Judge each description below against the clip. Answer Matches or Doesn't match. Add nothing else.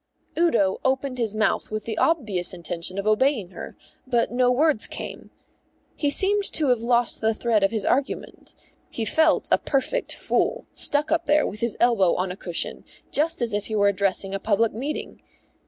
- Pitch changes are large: Matches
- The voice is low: Doesn't match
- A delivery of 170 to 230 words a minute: Matches